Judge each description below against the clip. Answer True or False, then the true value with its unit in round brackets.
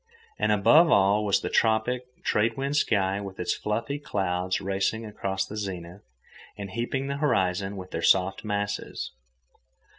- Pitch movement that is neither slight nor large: True (3.0 semitones)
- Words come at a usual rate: True (150 wpm)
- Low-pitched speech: True (100 Hz)